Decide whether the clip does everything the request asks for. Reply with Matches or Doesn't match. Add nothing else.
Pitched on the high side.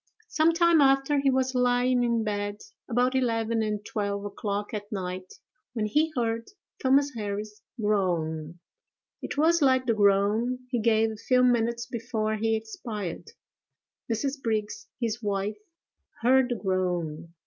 Matches